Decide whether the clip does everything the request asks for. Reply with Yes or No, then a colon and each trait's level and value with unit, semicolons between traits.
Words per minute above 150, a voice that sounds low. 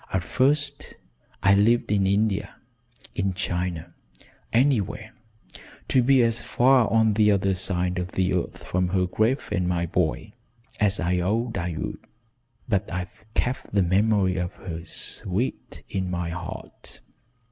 No: average, 145 wpm; very low, 95 Hz